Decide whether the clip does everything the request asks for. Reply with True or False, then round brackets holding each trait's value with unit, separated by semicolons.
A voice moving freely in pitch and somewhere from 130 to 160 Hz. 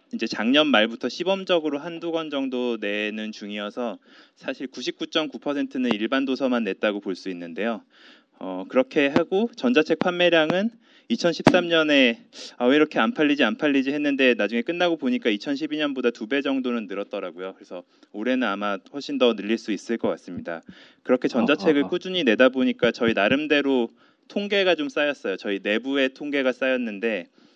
True (6.3 semitones; 135 Hz)